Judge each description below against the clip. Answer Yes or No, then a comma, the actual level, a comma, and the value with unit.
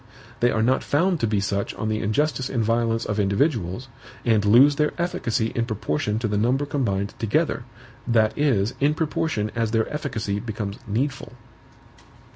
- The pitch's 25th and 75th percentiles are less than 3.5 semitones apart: No, average, 4.4 semitones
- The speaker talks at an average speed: Yes, average, 165 wpm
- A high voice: No, low, 115 Hz